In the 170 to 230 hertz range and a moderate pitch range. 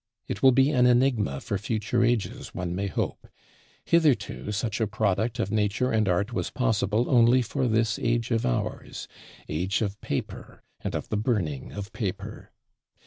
No: low, 110 Hz; average, 3.4 semitones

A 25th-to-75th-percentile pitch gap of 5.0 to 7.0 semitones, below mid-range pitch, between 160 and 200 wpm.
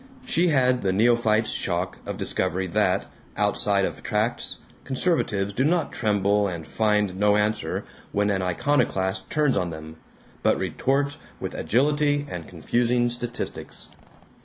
No: wide, 5.6 semitones; low, 105 Hz; slow, 135 wpm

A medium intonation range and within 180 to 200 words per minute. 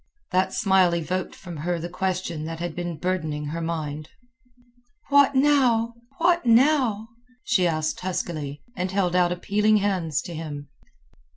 No: average, 4.3 semitones; average, 145 wpm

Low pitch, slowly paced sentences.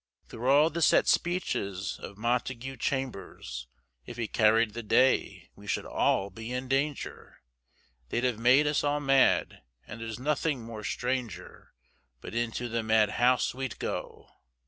No: low, 120 Hz; average, 145 wpm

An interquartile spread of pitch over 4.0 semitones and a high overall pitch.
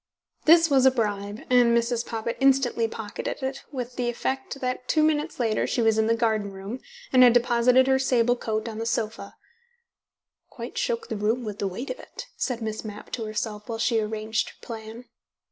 No: narrow, 2.6 semitones; high, 235 Hz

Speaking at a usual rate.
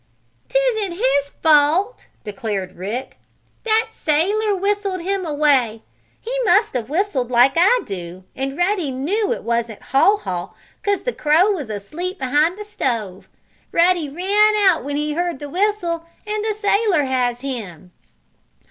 Yes: average, 145 wpm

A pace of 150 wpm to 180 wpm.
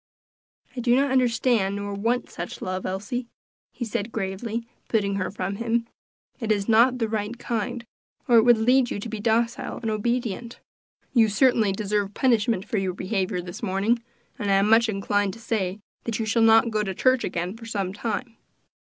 No: average, 190 wpm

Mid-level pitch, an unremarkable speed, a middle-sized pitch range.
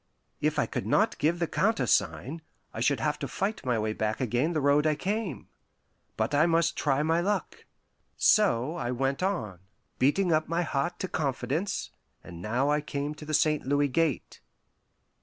Yes: medium, 150 Hz; average, 175 wpm; average, 4.4 semitones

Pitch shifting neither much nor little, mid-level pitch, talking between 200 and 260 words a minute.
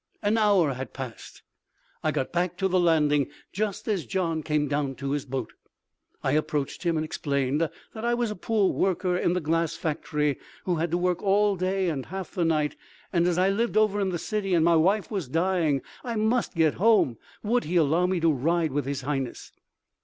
Yes: average, 4.5 semitones; medium, 170 Hz; fast, 205 wpm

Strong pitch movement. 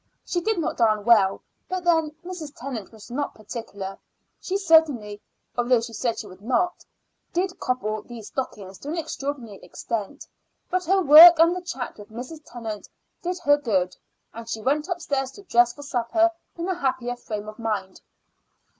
Yes: wide, 7.2 semitones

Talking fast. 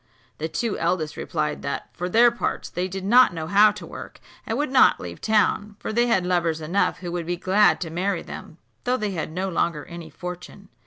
Yes: fast, 215 wpm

